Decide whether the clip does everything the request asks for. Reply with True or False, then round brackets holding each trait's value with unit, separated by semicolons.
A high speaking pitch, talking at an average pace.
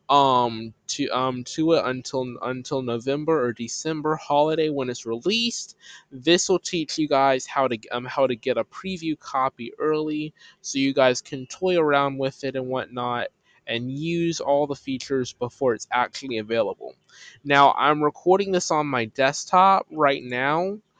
False (135 Hz; 165 wpm)